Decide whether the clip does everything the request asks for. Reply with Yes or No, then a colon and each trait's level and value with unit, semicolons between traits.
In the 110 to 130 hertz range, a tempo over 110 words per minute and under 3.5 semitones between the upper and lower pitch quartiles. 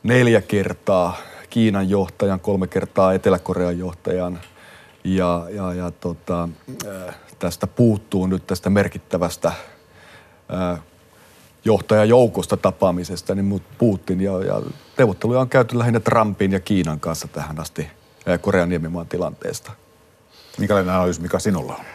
No: very low, 95 Hz; average, 120 wpm; average, 2.8 semitones